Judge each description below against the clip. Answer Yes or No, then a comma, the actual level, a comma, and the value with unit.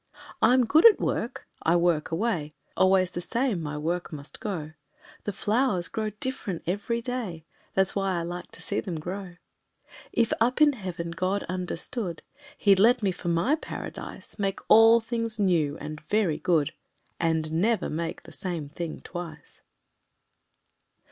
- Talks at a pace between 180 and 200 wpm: No, average, 155 wpm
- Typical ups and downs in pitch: Yes, average, 4.8 semitones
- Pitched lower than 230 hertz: Yes, medium, 185 Hz